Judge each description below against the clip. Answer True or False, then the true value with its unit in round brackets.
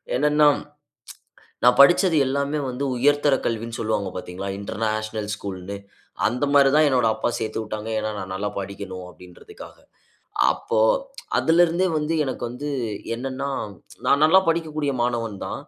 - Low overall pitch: True (125 Hz)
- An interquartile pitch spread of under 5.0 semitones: False (5.4 semitones)